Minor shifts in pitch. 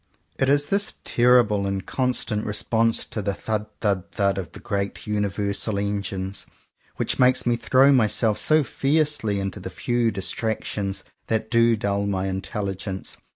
No: average, 3.3 semitones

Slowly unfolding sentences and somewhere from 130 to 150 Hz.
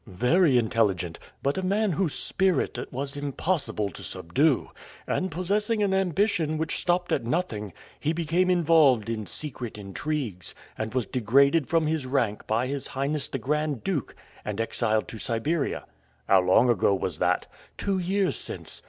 No: average, 160 wpm; medium, 140 Hz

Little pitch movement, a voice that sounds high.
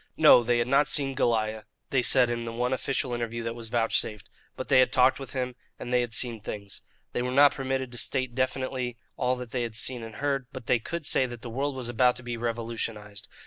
No: narrow, 2.0 semitones; low, 120 Hz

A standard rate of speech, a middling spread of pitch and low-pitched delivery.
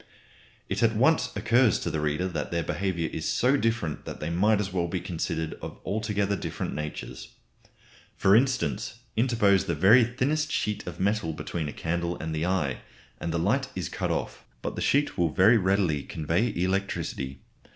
Yes: average, 180 wpm; average, 5.0 semitones; very low, 95 Hz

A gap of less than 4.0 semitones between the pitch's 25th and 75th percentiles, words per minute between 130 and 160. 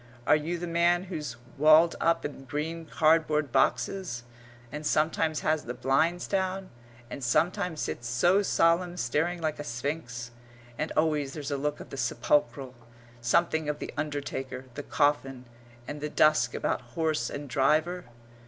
Yes: average, 3.6 semitones; average, 155 wpm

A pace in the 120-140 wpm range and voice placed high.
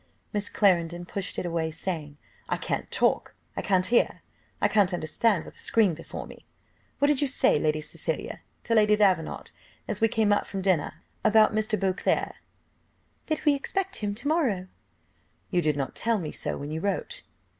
No: average, 180 wpm; high, 200 Hz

